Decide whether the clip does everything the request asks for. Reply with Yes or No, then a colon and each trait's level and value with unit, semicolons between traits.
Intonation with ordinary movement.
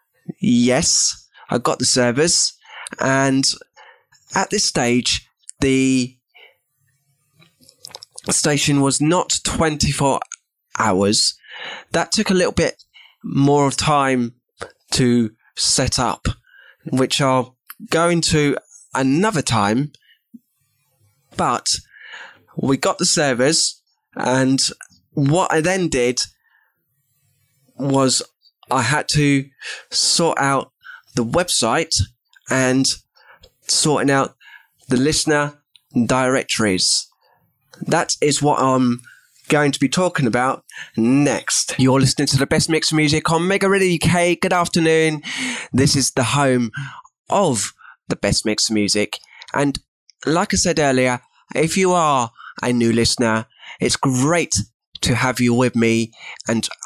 Yes: average, 4.1 semitones